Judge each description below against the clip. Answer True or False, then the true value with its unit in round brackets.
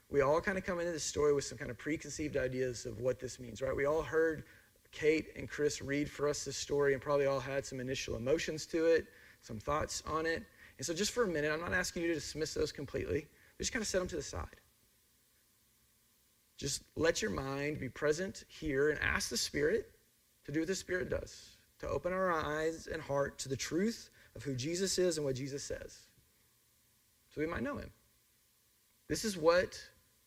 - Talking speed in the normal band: False (210 wpm)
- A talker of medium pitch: True (150 Hz)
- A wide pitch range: False (4.1 semitones)